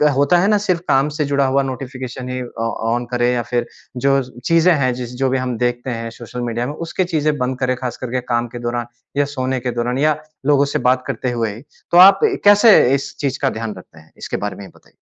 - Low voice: Yes, low, 130 Hz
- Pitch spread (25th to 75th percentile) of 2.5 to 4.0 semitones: Yes, average, 2.8 semitones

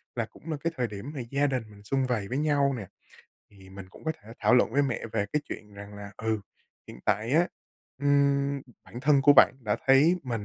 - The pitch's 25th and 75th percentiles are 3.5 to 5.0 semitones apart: No, wide, 5.4 semitones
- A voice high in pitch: No, low, 125 Hz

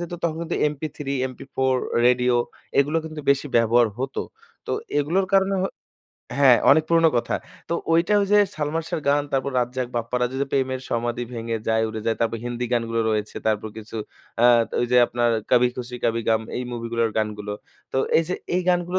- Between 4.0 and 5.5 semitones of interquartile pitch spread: Yes, average, 4.6 semitones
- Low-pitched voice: Yes, low, 125 Hz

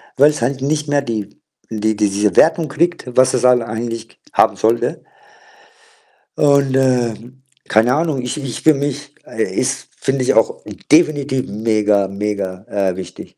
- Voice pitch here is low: Yes, low, 125 Hz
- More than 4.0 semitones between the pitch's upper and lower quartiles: Yes, average, 4.9 semitones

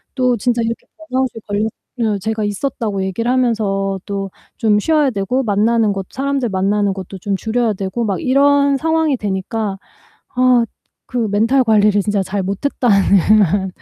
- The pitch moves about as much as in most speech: Yes, average, 4.0 semitones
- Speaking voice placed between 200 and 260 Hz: Yes, high, 215 Hz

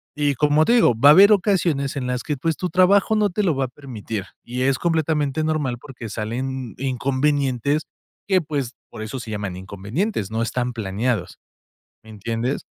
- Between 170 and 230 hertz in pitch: No, low, 135 Hz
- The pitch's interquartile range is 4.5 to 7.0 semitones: Yes, average, 5.1 semitones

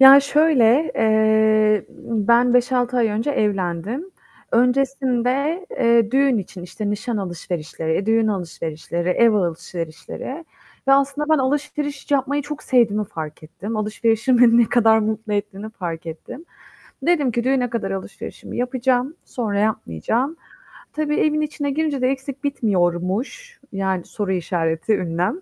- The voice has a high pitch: Yes, high, 230 Hz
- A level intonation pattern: No, wide, 5.4 semitones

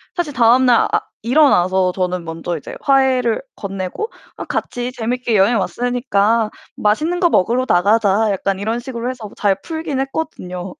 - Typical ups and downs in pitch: Yes, average, 5.0 semitones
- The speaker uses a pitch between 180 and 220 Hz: No, high, 230 Hz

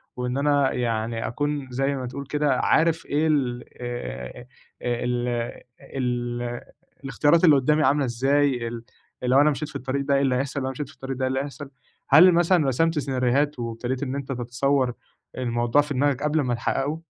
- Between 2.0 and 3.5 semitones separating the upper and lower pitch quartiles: Yes, average, 2.9 semitones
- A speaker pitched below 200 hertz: Yes, low, 135 Hz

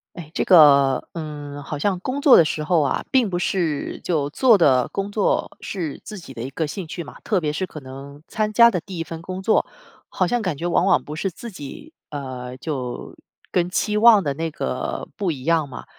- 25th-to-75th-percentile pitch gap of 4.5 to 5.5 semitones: Yes, average, 5.1 semitones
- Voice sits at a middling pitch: Yes, medium, 165 Hz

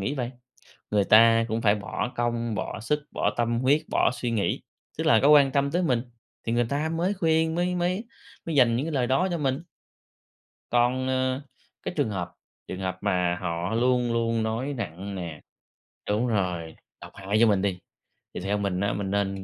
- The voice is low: Yes, low, 115 Hz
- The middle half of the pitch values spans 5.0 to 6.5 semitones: Yes, average, 5.3 semitones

